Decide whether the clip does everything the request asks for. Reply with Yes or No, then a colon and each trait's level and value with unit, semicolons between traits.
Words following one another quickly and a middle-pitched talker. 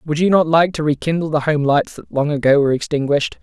Yes: fast, 245 wpm; medium, 150 Hz